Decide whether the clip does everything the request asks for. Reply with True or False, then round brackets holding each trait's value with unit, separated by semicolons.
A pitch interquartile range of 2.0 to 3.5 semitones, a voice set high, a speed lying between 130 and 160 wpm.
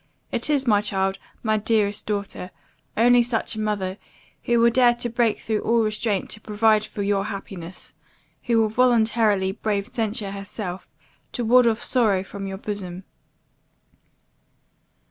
True (2.7 semitones; 215 Hz; 145 wpm)